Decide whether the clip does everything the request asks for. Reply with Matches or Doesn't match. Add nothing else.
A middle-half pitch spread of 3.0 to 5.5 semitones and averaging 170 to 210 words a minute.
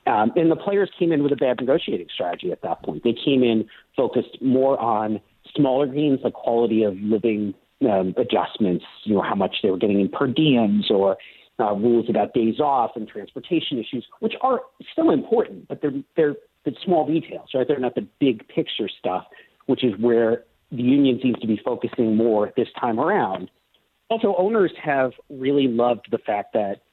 Matches